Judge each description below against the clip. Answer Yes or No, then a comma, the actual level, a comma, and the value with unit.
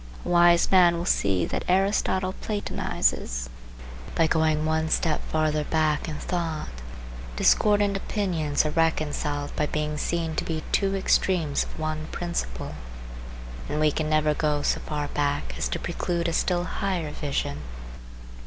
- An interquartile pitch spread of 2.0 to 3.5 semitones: Yes, narrow, 2.6 semitones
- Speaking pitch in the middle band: Yes, medium, 155 Hz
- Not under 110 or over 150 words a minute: Yes, average, 145 wpm